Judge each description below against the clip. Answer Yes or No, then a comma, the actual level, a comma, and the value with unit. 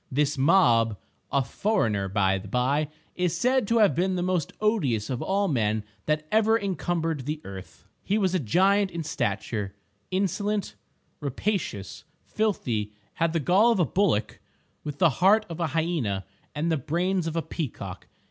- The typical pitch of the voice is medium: Yes, medium, 160 Hz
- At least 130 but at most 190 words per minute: Yes, average, 160 wpm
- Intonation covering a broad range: Yes, wide, 8.4 semitones